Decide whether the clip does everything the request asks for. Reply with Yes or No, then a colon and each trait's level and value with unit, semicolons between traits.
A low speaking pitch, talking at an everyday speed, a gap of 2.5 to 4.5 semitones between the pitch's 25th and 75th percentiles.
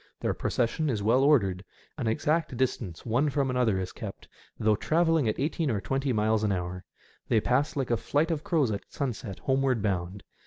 No: low, 120 Hz; average, 190 wpm; average, 5.3 semitones